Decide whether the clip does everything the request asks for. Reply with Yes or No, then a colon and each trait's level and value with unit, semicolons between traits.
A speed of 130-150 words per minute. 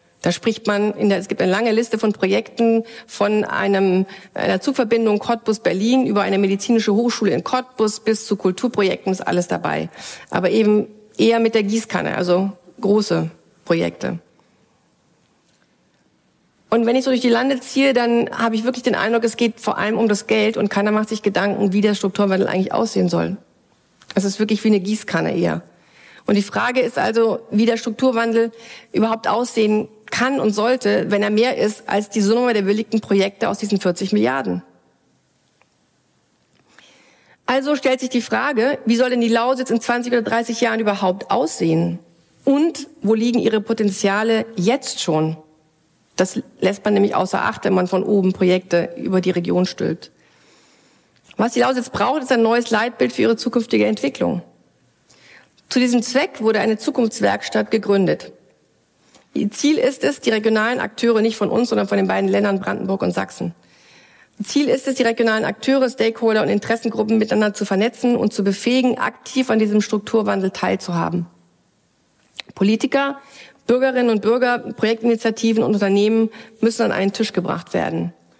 No: average, 160 wpm